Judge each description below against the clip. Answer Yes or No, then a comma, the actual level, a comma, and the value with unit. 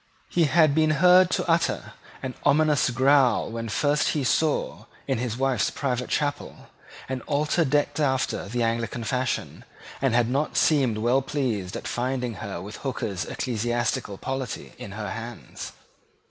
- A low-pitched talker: Yes, low, 130 Hz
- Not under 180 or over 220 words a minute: No, average, 150 wpm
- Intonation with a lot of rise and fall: No, average, 3.9 semitones